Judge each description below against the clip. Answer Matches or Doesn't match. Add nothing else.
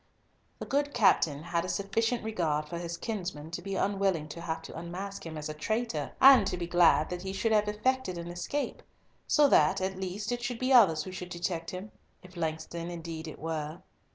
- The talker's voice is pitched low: Doesn't match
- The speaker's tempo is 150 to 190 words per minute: Doesn't match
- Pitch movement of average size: Matches